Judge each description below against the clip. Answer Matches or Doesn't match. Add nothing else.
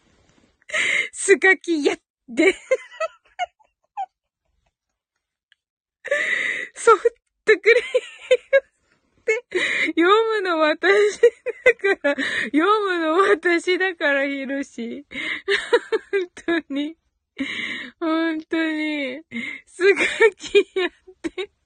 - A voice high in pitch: Matches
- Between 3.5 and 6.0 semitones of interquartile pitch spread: Matches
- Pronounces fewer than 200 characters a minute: Matches